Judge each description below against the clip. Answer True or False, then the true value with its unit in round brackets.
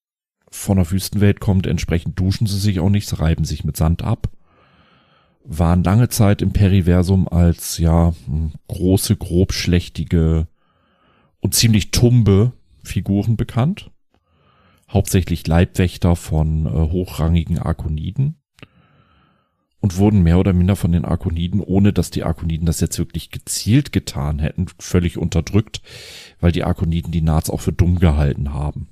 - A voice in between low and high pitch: False (90 Hz)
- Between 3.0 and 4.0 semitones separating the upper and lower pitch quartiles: True (3.4 semitones)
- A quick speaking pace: False (135 wpm)